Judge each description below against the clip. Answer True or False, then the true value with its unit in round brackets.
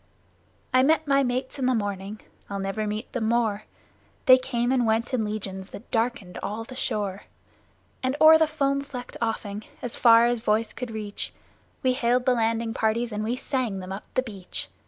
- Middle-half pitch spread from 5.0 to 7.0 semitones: False (3.3 semitones)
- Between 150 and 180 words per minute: False (190 wpm)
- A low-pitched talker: False (230 Hz)